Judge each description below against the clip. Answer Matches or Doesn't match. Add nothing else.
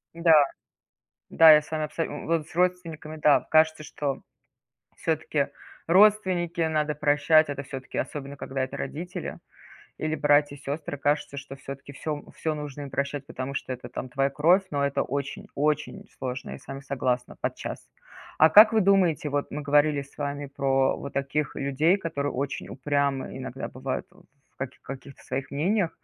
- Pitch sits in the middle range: Matches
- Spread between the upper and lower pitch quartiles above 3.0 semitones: Doesn't match